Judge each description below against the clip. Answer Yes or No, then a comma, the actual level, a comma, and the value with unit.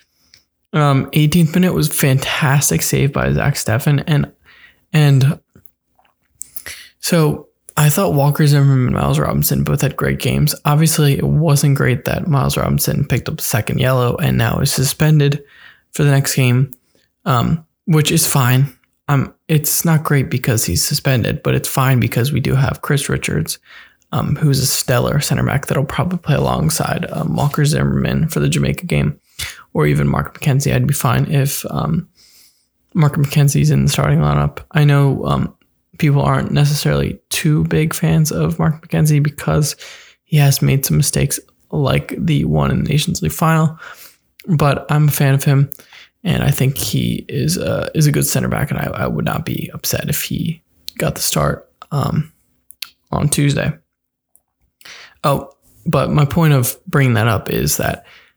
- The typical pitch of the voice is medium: Yes, medium, 145 Hz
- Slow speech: No, average, 170 wpm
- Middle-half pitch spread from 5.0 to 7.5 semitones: No, average, 2.7 semitones